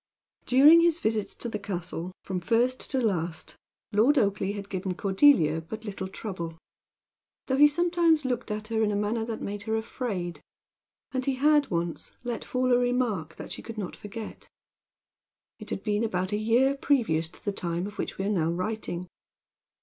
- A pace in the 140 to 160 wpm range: No, average, 180 wpm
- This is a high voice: Yes, high, 215 Hz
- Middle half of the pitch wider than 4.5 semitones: Yes, average, 5.1 semitones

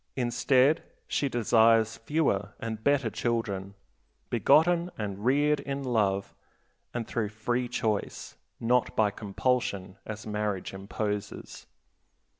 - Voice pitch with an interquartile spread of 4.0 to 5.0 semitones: No, average, 3.5 semitones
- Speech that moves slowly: Yes, slow, 105 wpm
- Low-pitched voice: Yes, low, 115 Hz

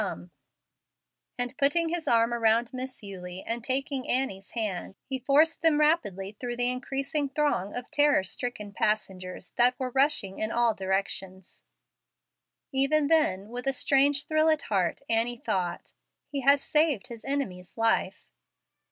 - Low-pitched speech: No, high, 245 Hz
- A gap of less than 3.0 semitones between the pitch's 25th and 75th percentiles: No, wide, 5.6 semitones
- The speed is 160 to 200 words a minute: No, average, 145 wpm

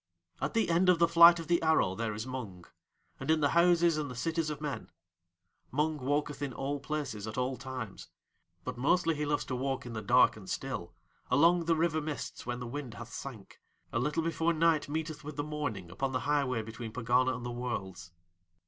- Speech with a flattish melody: No, average, 4.6 semitones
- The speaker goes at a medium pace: No, fast, 210 wpm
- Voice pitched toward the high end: No, medium, 140 Hz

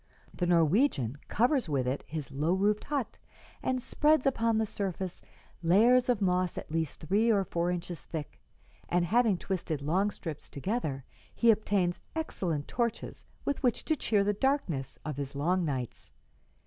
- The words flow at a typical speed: Yes, average, 160 wpm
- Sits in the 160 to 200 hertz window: Yes, medium, 185 Hz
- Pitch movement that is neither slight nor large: No, wide, 6.4 semitones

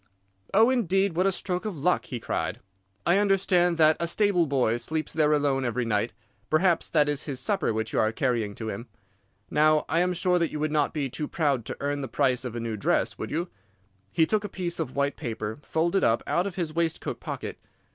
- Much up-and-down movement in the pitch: Yes, wide, 5.8 semitones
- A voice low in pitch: No, medium, 155 Hz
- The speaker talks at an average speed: No, fast, 220 wpm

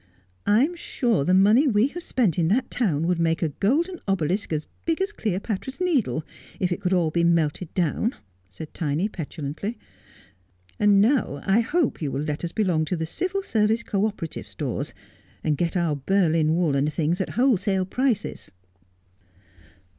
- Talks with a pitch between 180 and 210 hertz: Yes, medium, 185 Hz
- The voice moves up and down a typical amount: No, wide, 6.2 semitones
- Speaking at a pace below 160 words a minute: No, average, 175 wpm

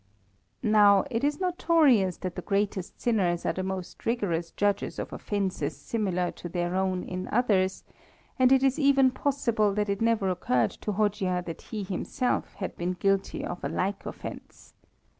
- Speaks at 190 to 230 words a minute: No, average, 165 wpm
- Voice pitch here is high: Yes, high, 200 Hz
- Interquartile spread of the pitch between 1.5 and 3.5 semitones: No, average, 3.9 semitones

